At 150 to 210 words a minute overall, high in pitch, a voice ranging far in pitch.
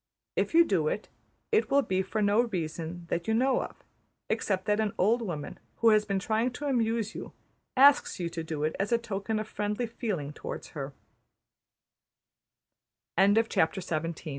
No: average, 160 wpm; high, 210 Hz; average, 4.3 semitones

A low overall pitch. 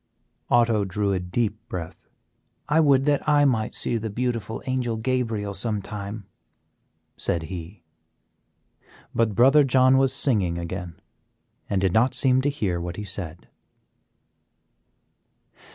Yes: low, 110 Hz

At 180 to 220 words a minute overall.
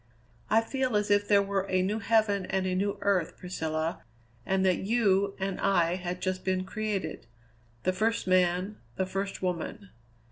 No: average, 170 wpm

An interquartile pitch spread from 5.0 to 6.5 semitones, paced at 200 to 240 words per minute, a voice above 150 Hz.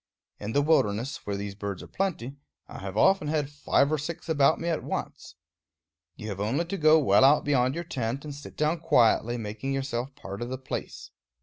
No: average, 5.3 semitones; fast, 205 wpm; low, 135 Hz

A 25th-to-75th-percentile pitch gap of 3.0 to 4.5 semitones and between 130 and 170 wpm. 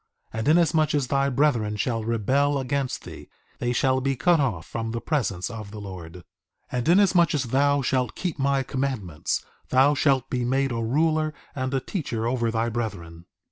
No: average, 3.9 semitones; average, 185 wpm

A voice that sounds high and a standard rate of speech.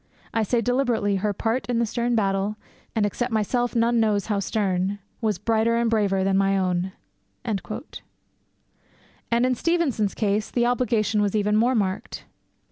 Yes: high, 215 Hz; average, 155 wpm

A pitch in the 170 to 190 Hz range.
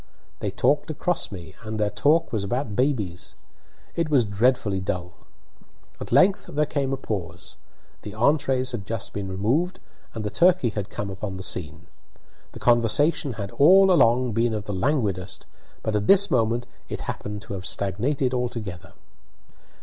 No: low, 115 Hz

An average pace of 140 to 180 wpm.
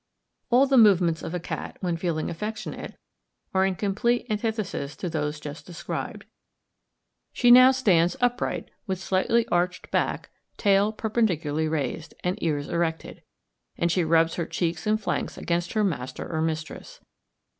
Yes: average, 145 wpm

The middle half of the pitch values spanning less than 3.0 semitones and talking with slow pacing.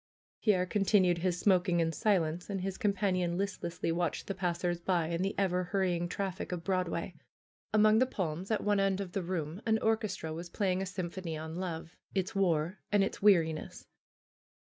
No: narrow, 2.4 semitones; average, 185 wpm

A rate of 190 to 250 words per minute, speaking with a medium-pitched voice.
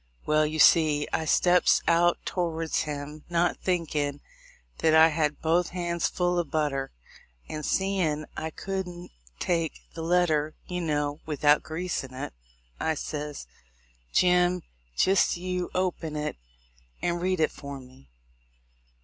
No: slow, 135 wpm; medium, 160 Hz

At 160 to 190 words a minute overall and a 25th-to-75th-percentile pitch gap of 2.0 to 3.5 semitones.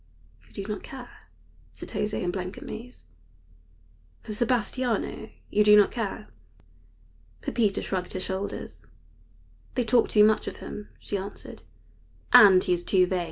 No: average, 145 wpm; average, 2.9 semitones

